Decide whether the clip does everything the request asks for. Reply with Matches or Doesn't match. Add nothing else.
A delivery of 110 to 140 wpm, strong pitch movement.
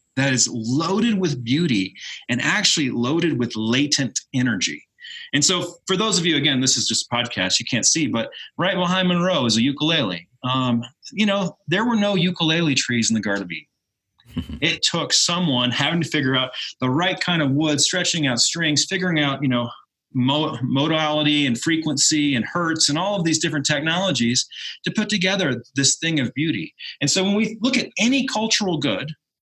Doesn't match